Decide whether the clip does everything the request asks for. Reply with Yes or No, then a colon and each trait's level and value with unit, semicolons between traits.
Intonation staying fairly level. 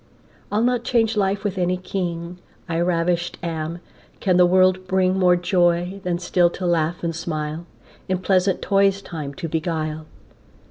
Yes: narrow, 1.9 semitones